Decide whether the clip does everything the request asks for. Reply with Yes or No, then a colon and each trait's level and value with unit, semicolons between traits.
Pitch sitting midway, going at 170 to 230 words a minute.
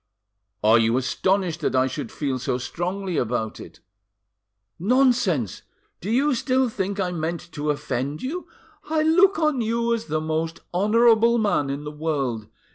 No: medium, 175 Hz; average, 155 wpm